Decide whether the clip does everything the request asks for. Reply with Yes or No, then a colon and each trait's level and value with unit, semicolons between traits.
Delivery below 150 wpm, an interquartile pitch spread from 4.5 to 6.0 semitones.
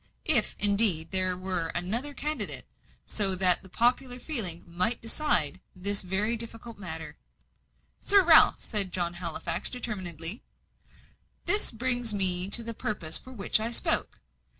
Yes: average, 140 wpm; average, 4.8 semitones